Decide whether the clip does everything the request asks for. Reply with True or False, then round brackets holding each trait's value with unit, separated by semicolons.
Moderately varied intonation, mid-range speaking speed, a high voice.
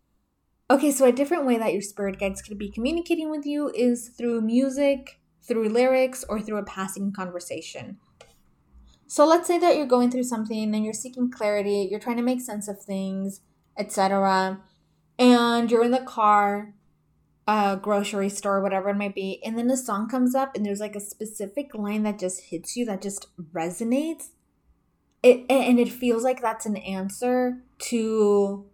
True (3.9 semitones; 180 wpm; 215 Hz)